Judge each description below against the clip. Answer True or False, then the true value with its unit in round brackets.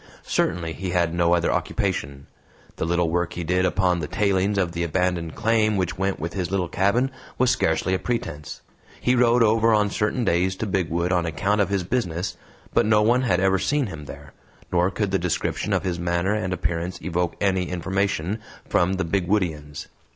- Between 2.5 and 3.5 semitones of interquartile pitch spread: True (2.9 semitones)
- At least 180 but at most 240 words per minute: True (190 wpm)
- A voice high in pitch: False (90 Hz)